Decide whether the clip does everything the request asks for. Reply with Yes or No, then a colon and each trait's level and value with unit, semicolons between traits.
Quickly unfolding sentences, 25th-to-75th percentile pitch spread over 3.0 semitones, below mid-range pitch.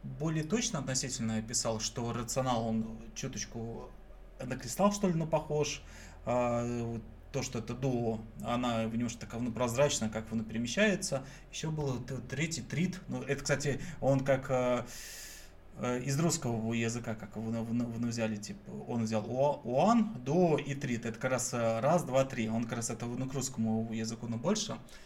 Yes: fast, 175 wpm; average, 3.6 semitones; low, 120 Hz